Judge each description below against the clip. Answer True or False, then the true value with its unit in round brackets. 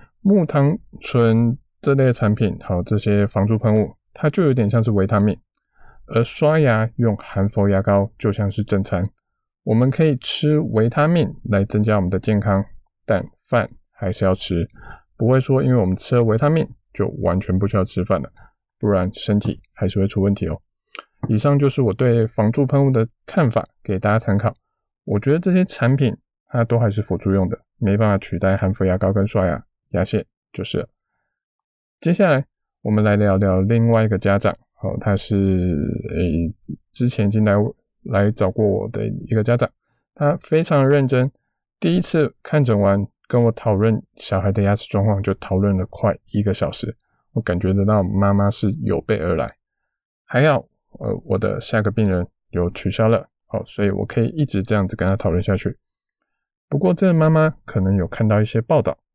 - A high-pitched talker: False (105 Hz)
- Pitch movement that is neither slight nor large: True (3.8 semitones)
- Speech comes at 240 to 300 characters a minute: True (265 characters per minute)